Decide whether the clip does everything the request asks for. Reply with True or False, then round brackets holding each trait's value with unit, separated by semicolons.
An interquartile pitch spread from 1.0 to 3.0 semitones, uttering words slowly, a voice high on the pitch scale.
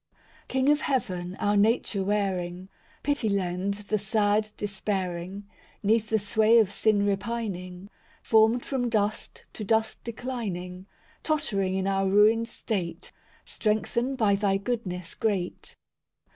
True (2.7 semitones; 125 wpm; 205 Hz)